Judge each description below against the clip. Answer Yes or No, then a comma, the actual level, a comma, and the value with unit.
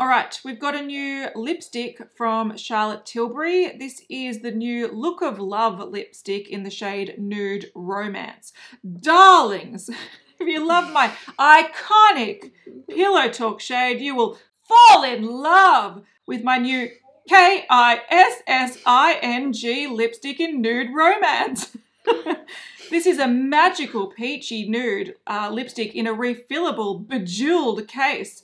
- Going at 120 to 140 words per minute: Yes, slow, 135 wpm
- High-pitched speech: Yes, very high, 250 Hz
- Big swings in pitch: Yes, wide, 6.2 semitones